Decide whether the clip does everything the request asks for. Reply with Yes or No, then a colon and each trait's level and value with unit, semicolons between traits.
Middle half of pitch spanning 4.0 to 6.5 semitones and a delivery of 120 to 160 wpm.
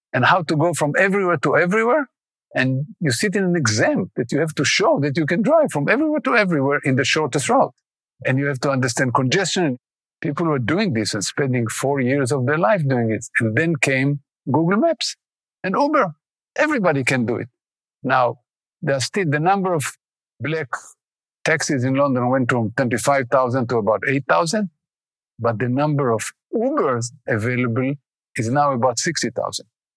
No: average, 4.3 semitones; average, 180 wpm